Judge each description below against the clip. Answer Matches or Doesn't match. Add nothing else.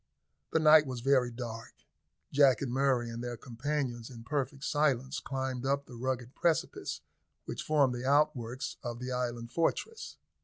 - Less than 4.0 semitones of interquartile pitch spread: Matches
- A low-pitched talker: Matches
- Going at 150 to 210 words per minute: Matches